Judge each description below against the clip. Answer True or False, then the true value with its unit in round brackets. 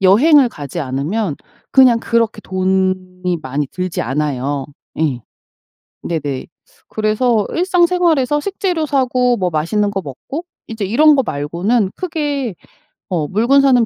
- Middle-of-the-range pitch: False (210 Hz)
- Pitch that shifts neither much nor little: False (8.1 semitones)